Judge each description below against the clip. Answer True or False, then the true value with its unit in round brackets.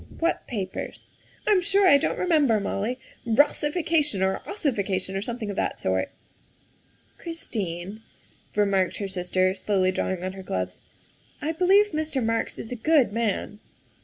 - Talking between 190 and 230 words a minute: False (155 wpm)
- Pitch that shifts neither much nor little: False (8.0 semitones)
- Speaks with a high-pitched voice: True (220 Hz)